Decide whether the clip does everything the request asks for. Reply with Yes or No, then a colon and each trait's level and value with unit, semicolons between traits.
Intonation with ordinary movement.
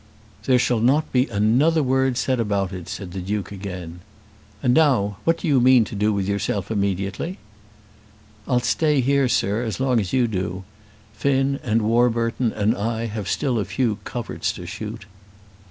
Yes: average, 4.4 semitones